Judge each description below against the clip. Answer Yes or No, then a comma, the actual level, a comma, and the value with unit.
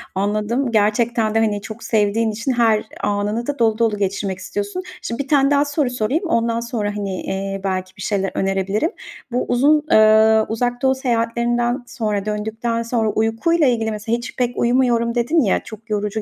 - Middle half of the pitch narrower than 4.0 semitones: Yes, narrow, 2.6 semitones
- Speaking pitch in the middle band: No, high, 225 Hz